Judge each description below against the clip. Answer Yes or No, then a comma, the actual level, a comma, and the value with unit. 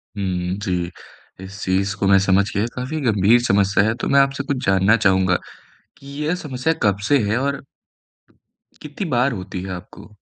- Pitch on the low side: Yes, low, 105 Hz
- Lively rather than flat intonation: Yes, wide, 6.1 semitones